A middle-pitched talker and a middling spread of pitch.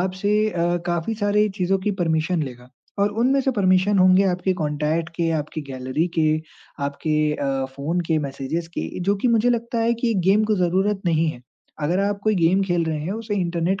Yes: medium, 180 Hz; average, 4.4 semitones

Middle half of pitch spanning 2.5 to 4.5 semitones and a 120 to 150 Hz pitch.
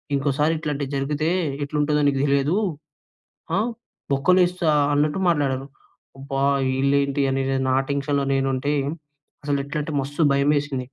No: narrow, 1.5 semitones; medium, 140 Hz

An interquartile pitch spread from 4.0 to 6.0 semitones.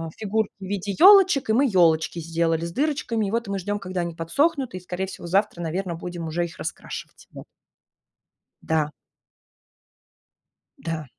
Yes: average, 4.6 semitones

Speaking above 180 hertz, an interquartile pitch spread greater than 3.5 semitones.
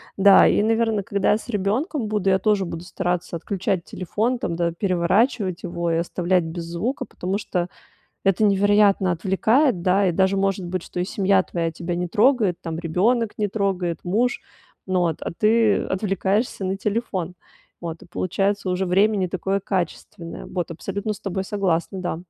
No: high, 190 Hz; average, 2.7 semitones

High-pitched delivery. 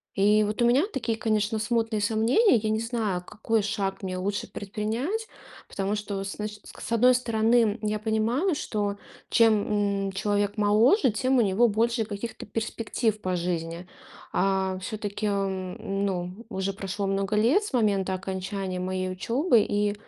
Yes: high, 210 Hz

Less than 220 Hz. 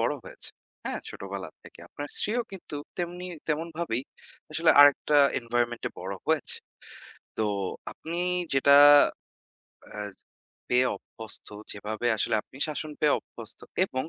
Yes: low, 135 Hz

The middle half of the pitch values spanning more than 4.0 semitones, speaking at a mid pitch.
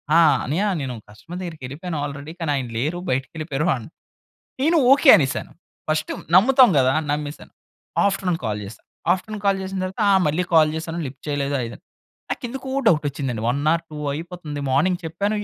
Yes: average, 4.8 semitones; medium, 160 Hz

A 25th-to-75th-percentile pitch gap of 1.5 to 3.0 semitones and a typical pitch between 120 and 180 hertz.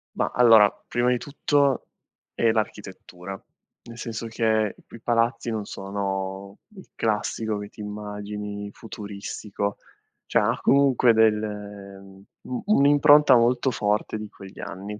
No: average, 2.7 semitones; low, 105 Hz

